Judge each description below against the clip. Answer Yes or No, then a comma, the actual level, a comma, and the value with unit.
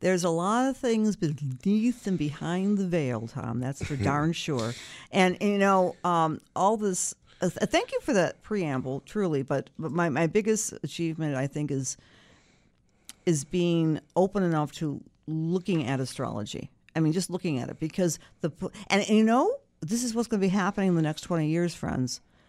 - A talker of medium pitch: Yes, medium, 170 Hz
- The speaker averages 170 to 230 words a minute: Yes, average, 190 wpm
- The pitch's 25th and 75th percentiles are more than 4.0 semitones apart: Yes, average, 5.2 semitones